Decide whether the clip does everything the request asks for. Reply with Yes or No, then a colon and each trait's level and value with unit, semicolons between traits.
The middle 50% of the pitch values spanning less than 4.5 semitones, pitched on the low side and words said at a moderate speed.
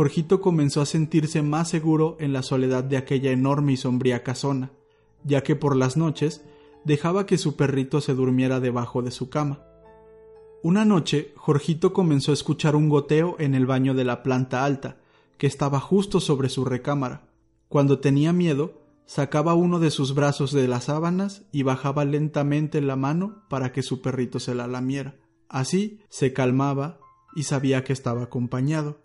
No: average, 2.8 semitones; medium, 145 Hz; average, 170 wpm